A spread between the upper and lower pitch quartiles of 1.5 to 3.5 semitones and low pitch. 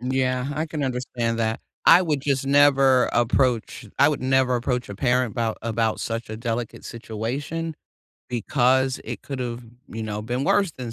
Yes: average, 2.9 semitones; low, 125 Hz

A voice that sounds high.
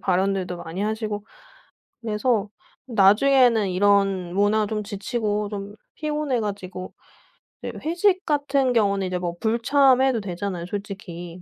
Yes: high, 205 Hz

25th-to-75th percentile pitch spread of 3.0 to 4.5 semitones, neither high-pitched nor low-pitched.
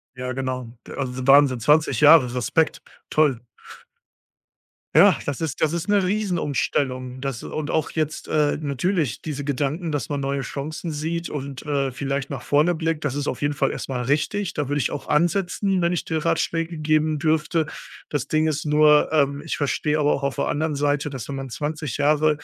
No: narrow, 2.4 semitones; medium, 150 Hz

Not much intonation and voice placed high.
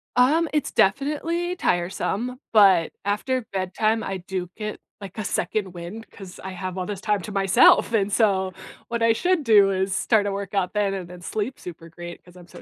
No: average, 3.3 semitones; high, 200 Hz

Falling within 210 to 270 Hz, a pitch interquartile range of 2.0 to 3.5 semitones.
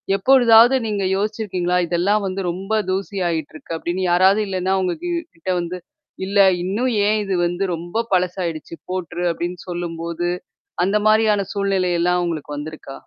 No: medium, 185 Hz; average, 2.8 semitones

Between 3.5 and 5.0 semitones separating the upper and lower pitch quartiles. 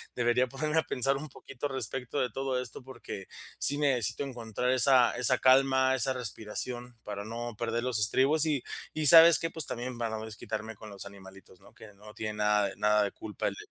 Yes: average, 3.8 semitones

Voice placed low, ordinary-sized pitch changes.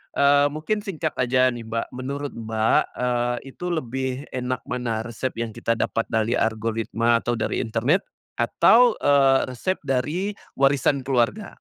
Yes: low, 130 Hz; average, 3.6 semitones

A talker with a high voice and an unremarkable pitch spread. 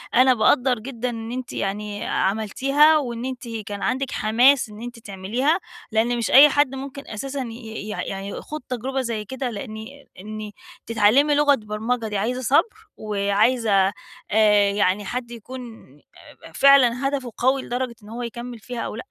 Yes: high, 240 Hz; average, 3.6 semitones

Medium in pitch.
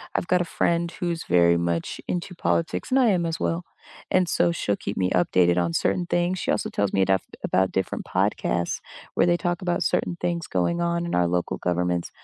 Yes: medium, 165 Hz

